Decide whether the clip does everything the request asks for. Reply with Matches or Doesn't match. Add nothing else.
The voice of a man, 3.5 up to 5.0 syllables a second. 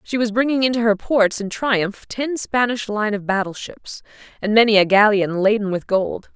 Doesn't match